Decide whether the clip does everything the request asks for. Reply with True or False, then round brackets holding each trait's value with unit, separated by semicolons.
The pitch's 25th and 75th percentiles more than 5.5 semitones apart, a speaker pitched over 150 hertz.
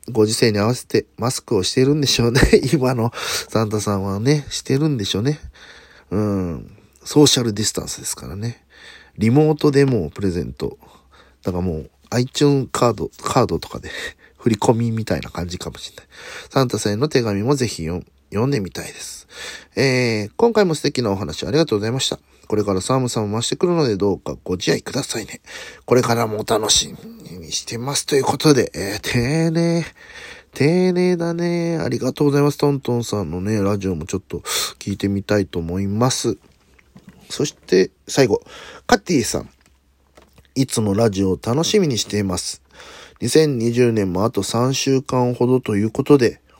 False (6.3 semitones; 115 Hz)